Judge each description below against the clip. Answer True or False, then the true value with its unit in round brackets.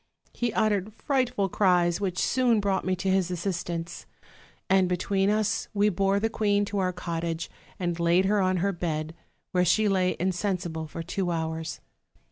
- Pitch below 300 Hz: True (185 Hz)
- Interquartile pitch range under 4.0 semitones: True (2.8 semitones)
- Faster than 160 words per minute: True (170 wpm)